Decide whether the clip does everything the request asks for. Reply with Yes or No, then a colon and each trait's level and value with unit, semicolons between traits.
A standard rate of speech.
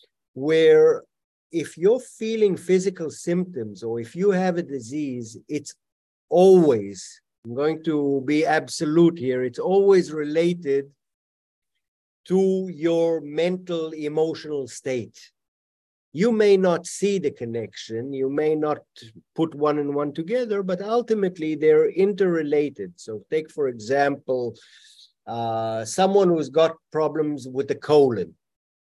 No: slow, 120 wpm